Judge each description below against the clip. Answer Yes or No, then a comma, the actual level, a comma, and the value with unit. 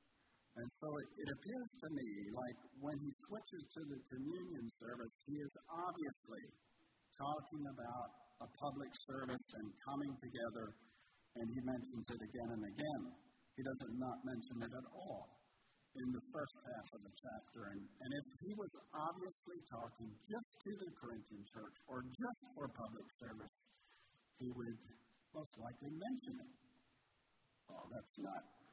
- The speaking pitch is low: Yes, low, 130 Hz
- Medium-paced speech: Yes, average, 155 wpm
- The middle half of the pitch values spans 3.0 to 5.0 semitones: Yes, average, 4.5 semitones